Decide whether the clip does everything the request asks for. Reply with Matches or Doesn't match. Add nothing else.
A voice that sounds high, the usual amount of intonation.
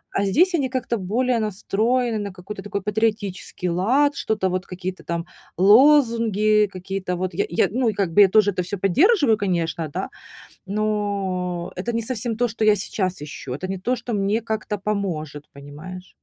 Matches